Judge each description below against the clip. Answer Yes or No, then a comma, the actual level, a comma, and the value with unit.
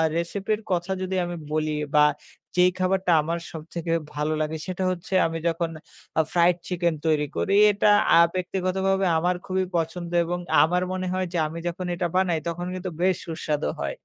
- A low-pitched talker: No, medium, 175 Hz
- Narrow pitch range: Yes, narrow, 2.0 semitones